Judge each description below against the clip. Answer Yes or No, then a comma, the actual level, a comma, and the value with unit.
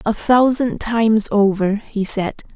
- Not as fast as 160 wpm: Yes, average, 140 wpm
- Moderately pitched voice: No, high, 215 Hz